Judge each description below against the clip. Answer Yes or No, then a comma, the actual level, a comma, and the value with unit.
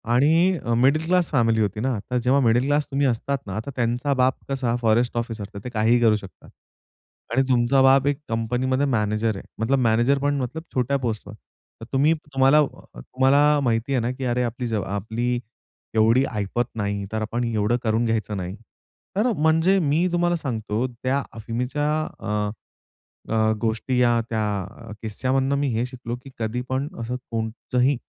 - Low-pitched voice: Yes, low, 120 Hz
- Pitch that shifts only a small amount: No, average, 3.4 semitones